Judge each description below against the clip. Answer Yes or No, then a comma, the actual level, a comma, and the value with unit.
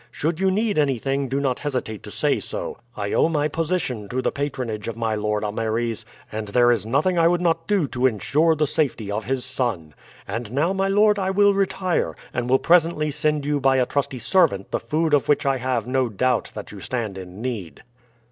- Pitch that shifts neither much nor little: No, wide, 5.9 semitones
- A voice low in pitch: Yes, low, 130 Hz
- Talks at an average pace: No, fast, 215 wpm